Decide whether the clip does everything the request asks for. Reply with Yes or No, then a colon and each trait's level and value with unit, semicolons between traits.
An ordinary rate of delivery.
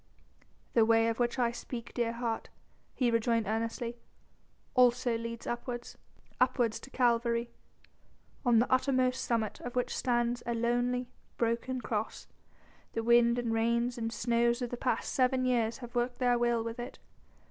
Yes: average, 155 wpm